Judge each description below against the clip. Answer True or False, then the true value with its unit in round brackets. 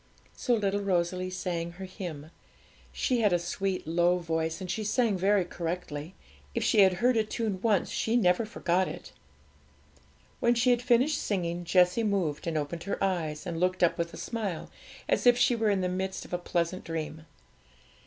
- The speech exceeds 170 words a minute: True (185 wpm)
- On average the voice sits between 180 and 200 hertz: True (185 Hz)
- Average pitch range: True (3.7 semitones)